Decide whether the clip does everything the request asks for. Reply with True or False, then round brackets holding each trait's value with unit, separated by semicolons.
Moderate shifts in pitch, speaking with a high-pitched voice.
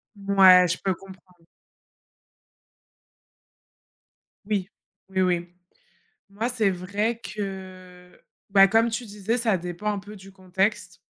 False (2.3 semitones; 195 Hz)